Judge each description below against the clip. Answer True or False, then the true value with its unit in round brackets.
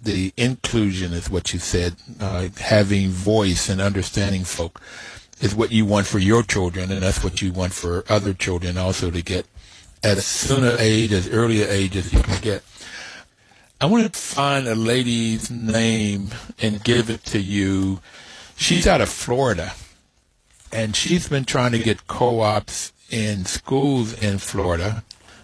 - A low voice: True (105 Hz)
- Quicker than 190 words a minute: False (165 wpm)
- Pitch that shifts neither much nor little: True (3.2 semitones)